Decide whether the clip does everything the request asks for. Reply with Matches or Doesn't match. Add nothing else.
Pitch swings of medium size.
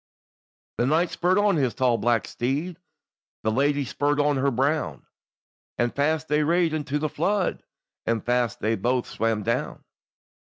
Matches